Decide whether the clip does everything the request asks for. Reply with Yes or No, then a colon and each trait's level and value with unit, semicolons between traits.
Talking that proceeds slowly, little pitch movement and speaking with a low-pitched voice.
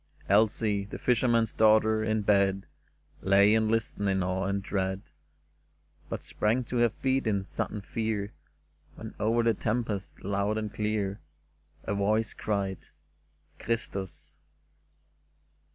Yes: slow, 130 wpm; narrow, 2.2 semitones; low, 105 Hz